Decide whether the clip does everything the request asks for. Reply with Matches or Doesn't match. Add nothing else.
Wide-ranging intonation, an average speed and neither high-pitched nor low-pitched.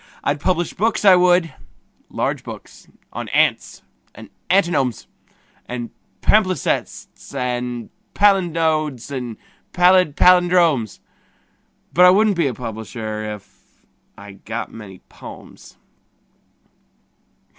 Doesn't match